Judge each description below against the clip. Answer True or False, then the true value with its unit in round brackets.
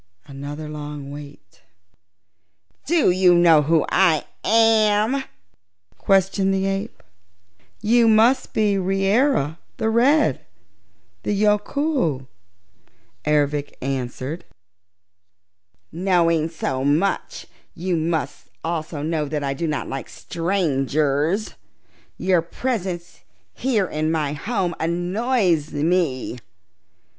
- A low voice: False (170 Hz)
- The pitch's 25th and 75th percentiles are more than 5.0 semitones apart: True (5.5 semitones)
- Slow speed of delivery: True (95 wpm)